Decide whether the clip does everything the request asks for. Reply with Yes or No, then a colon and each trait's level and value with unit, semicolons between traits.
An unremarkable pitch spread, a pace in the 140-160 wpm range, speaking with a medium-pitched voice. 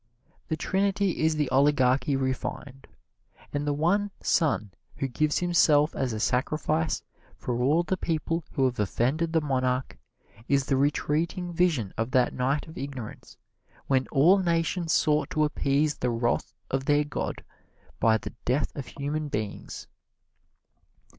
Yes: average, 3.5 semitones; average, 145 wpm; medium, 145 Hz